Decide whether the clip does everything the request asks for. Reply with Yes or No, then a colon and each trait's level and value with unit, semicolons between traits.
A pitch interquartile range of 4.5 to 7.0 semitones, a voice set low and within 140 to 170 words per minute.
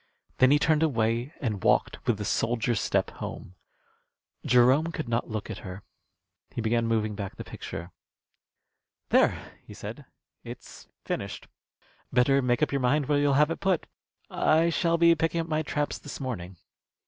Yes: average, 5.2 semitones; low, 130 Hz; average, 165 wpm